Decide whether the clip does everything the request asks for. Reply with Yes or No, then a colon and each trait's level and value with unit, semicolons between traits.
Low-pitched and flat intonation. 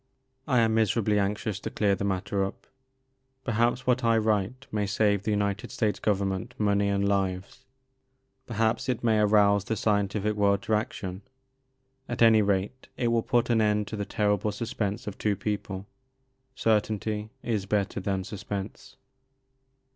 Yes: low, 105 Hz; narrow, 1.8 semitones